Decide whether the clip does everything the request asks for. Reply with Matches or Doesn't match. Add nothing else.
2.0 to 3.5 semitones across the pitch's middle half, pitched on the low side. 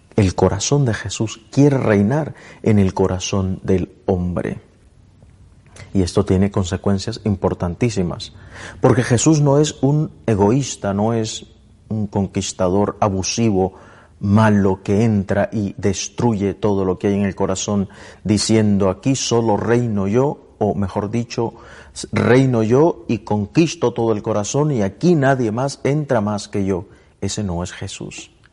Matches